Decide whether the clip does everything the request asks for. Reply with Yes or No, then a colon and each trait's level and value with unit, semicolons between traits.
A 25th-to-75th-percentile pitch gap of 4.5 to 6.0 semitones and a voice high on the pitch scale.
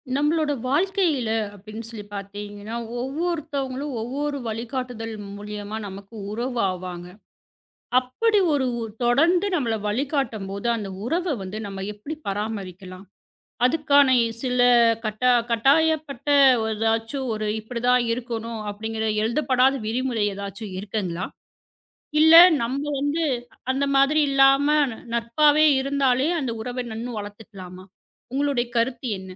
Yes: average, 4.9 semitones; high, 240 Hz